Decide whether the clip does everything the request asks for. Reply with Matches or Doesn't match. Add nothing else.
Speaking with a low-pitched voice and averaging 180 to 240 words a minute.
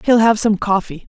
Doesn't match